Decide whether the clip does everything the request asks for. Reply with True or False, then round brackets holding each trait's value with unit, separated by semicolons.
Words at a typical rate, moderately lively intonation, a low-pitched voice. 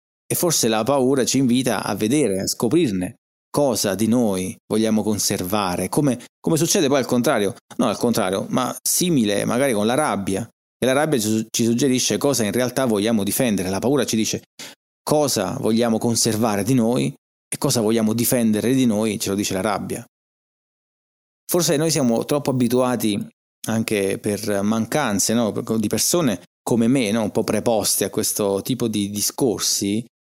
True (160 wpm; 3.0 semitones; 110 Hz)